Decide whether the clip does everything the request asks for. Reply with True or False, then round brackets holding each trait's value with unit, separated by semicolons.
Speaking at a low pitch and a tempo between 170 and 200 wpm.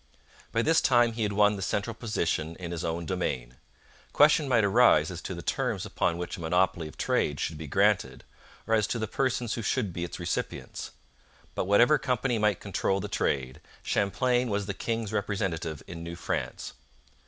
True (100 Hz; 190 wpm)